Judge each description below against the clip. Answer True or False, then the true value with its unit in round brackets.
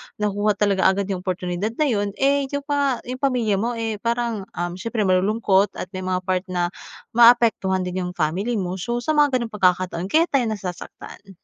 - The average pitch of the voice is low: False (205 Hz)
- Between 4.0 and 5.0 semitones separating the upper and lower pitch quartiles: True (4.5 semitones)